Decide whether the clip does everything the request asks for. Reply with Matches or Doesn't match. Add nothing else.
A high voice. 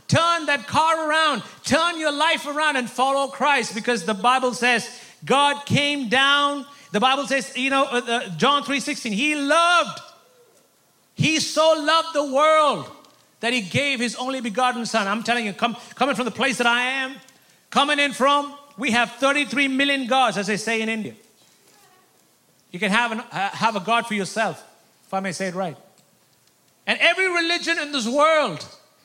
Matches